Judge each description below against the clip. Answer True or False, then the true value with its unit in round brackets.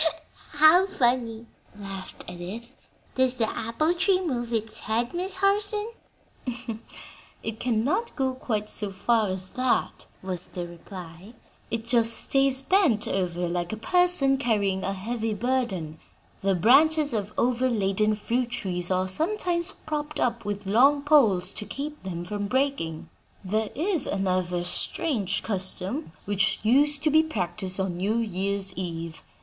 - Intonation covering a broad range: True (6.4 semitones)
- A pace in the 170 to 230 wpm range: False (140 wpm)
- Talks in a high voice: True (225 Hz)